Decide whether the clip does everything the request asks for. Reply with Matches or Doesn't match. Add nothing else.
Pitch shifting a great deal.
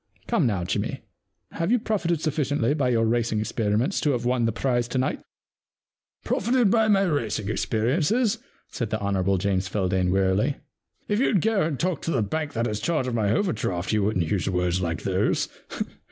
Matches